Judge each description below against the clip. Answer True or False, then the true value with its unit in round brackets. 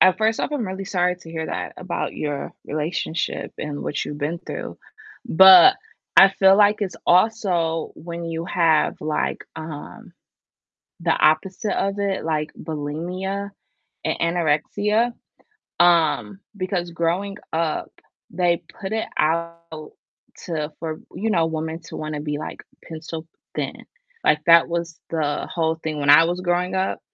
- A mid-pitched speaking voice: True (170 Hz)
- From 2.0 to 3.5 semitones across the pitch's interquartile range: True (3.1 semitones)